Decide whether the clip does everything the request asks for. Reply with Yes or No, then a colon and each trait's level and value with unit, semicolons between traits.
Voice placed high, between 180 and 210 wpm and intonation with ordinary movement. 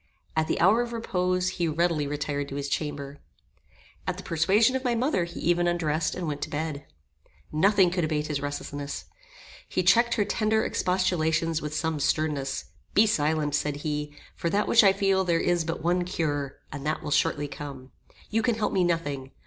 No: medium, 165 Hz; average, 190 wpm; average, 4.0 semitones